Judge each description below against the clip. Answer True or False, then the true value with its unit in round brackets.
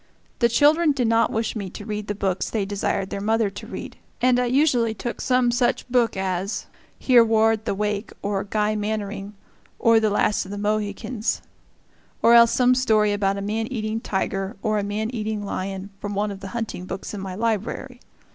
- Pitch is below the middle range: False (215 Hz)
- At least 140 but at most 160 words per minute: False (195 wpm)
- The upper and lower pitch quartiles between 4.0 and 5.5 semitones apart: False (2.5 semitones)